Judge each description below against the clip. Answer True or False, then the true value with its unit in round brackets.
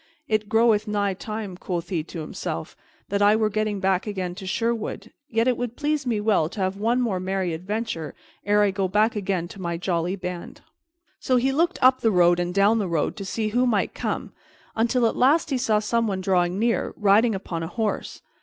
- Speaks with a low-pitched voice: False (205 Hz)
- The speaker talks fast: True (210 wpm)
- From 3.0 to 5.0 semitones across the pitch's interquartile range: True (3.5 semitones)